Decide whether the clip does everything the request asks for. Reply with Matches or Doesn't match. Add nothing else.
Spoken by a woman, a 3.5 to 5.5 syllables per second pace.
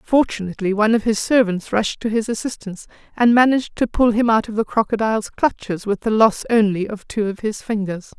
Doesn't match